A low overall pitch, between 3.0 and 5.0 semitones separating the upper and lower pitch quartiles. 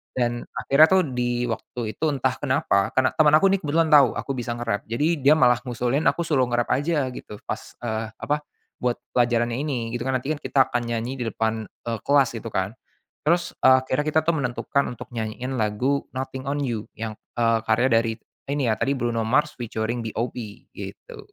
Yes: low, 125 Hz; average, 3.4 semitones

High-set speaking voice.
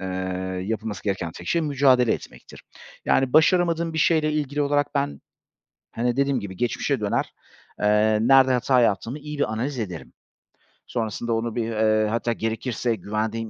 No: low, 120 Hz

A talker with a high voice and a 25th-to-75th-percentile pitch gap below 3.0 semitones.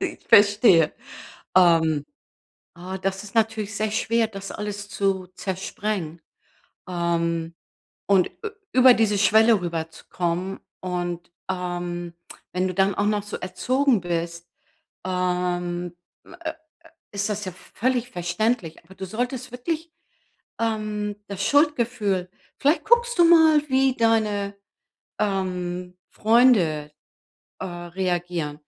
No: high, 195 Hz; average, 4.1 semitones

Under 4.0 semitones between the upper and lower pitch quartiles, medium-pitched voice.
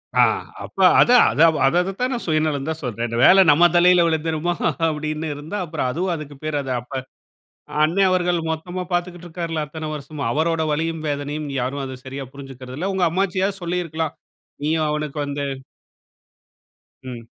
Yes: average, 3.4 semitones; medium, 160 Hz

